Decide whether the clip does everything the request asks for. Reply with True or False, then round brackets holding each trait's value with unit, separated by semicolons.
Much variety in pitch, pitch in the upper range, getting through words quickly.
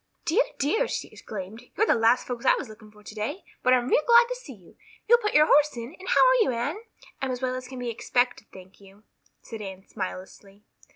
True (6.3 semitones; 245 Hz; 230 wpm)